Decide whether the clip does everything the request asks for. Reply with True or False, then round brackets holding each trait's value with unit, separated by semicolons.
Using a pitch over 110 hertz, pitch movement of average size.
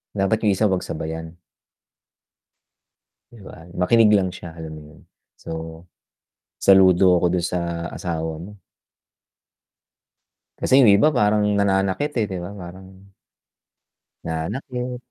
False (95 Hz; 3.5 semitones)